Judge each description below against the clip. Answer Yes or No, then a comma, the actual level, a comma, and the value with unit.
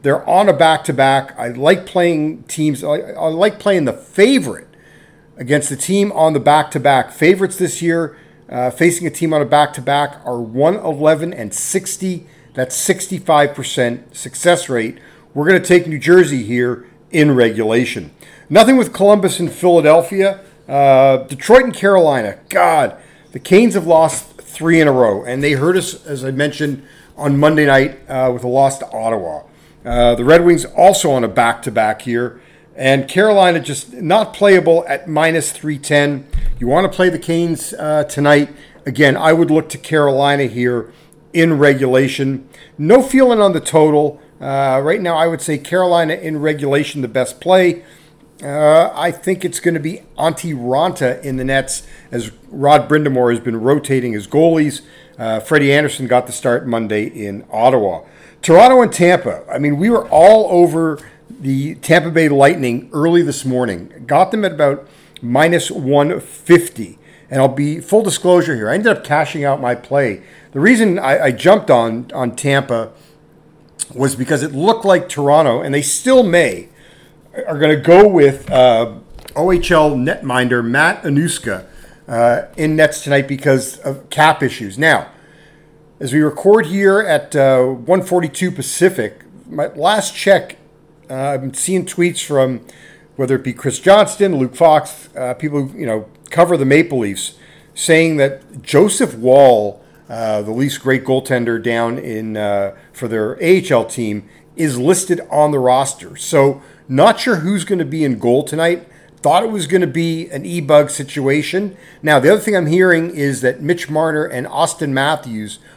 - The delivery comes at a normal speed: Yes, average, 170 wpm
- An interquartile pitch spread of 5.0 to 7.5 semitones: No, average, 4.3 semitones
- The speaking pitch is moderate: Yes, medium, 150 Hz